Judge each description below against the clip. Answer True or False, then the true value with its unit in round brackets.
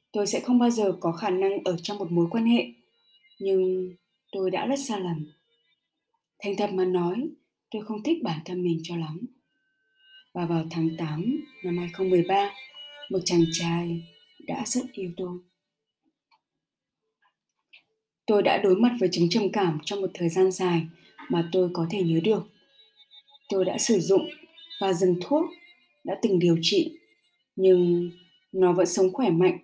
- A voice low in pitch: False (190 Hz)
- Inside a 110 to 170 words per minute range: True (165 wpm)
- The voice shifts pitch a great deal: True (6.8 semitones)